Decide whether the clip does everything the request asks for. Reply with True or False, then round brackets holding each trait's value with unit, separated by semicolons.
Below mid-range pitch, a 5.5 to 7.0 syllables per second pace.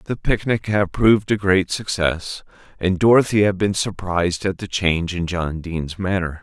False (95 Hz; 4.8 syllables/s)